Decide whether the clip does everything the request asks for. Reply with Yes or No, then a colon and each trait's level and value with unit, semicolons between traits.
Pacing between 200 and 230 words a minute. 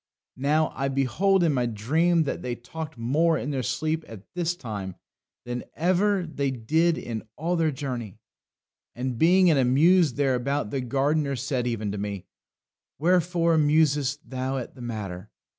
No: average, 160 wpm